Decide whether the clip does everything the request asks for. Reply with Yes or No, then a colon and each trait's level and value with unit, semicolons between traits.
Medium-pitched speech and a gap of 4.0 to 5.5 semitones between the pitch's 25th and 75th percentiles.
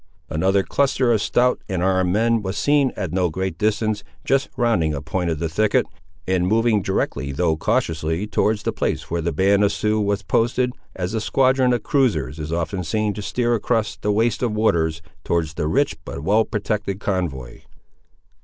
No: low, 100 Hz; average, 4.8 semitones